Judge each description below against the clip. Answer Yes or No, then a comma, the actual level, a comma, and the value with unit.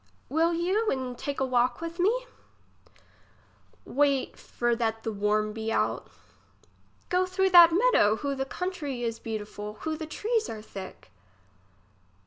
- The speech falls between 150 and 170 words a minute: No, average, 140 wpm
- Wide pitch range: Yes, wide, 7.8 semitones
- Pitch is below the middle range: No, very high, 275 Hz